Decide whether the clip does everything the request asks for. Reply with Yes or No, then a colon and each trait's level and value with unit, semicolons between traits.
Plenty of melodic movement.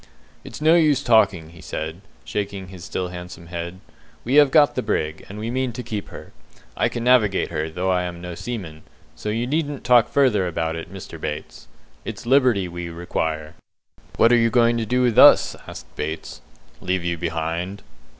Yes: wide, 6.1 semitones